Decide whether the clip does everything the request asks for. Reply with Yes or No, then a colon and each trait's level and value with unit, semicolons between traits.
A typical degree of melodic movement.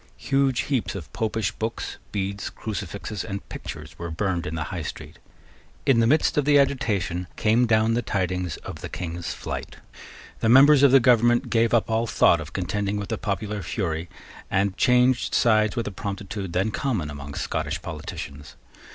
Yes: average, 4.6 semitones